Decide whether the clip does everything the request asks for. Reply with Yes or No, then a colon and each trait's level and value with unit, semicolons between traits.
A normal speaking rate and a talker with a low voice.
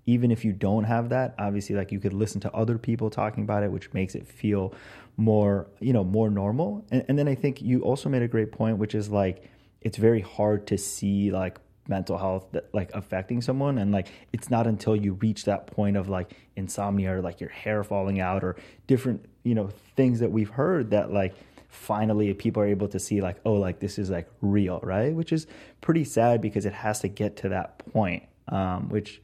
No: fast, 220 wpm; low, 105 Hz